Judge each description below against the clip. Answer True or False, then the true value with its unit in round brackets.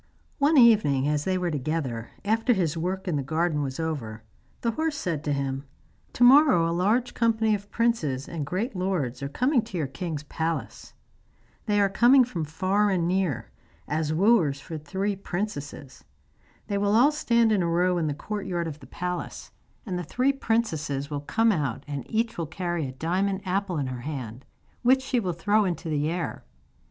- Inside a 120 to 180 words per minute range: False (190 wpm)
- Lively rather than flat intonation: True (6.4 semitones)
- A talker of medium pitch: True (175 Hz)